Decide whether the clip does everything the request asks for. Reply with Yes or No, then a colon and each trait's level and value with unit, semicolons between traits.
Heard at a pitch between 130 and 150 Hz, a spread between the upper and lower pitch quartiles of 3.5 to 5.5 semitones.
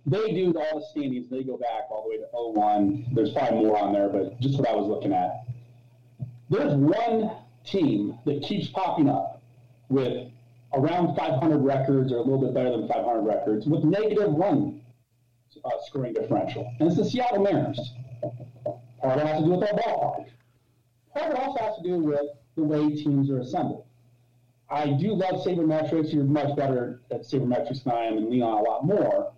Yes: low, 135 Hz; average, 4.0 semitones